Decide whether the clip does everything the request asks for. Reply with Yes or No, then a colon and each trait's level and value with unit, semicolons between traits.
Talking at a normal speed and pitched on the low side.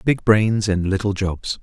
Yes: average, 185 wpm; low, 100 Hz